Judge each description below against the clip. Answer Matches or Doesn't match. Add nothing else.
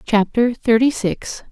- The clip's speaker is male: Doesn't match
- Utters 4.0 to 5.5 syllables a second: Doesn't match